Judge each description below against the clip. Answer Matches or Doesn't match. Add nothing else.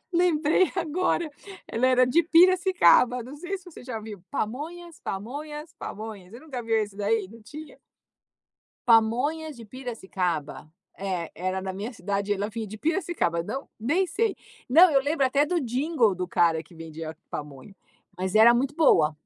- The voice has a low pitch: Doesn't match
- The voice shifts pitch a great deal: Matches